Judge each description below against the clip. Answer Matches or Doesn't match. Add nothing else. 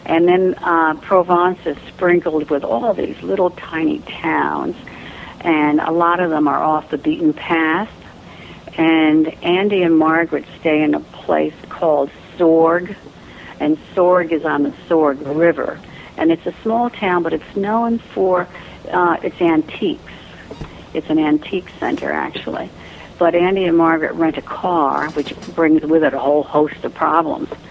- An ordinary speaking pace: Matches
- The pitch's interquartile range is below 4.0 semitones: Matches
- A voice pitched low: Doesn't match